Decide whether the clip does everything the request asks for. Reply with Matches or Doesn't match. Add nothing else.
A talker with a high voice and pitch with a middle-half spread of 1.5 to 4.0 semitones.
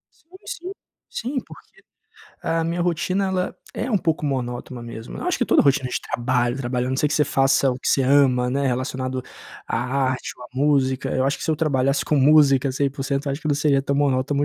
Doesn't match